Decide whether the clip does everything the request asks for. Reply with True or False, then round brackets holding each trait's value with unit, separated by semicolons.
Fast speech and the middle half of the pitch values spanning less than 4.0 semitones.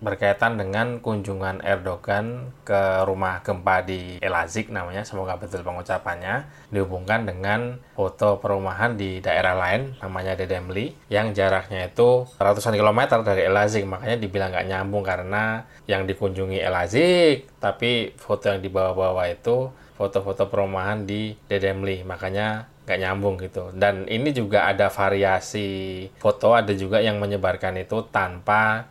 False (130 wpm; 2.4 semitones)